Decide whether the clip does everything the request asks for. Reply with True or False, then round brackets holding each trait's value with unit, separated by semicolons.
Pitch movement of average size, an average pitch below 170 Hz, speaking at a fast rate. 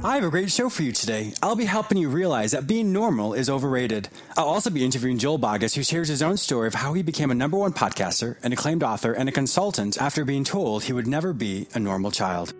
False (8.0 semitones; 140 Hz; 250 wpm)